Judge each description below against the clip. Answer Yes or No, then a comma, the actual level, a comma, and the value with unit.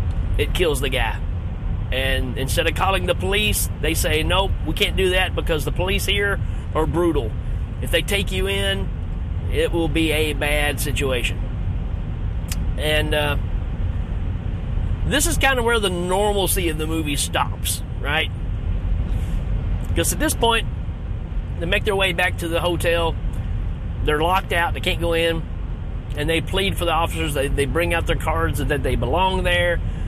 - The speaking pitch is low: Yes, very low, 90 Hz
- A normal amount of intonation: Yes, average, 3.0 semitones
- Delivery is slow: No, average, 165 wpm